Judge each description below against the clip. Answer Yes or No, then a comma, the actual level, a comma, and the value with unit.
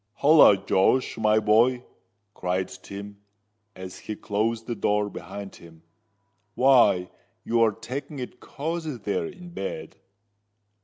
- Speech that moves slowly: Yes, slow, 120 wpm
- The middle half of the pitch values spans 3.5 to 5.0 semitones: Yes, average, 4.3 semitones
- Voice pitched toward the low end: Yes, low, 110 Hz